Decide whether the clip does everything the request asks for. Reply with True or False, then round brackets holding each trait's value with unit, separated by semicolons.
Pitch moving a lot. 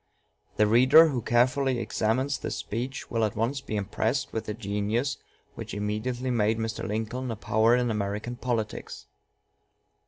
False (2.9 semitones)